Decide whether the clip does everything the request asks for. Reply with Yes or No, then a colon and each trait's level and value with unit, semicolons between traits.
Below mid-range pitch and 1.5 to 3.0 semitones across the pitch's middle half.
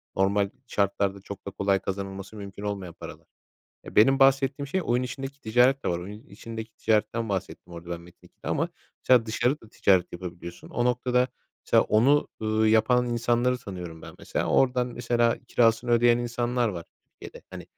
No: low, 110 Hz; average, 3.9 semitones